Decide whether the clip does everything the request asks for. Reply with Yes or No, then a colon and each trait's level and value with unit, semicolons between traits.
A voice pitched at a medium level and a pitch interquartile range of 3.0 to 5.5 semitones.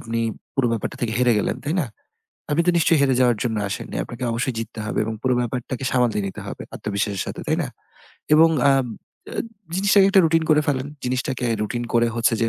No: low, 125 Hz; average, 3.9 semitones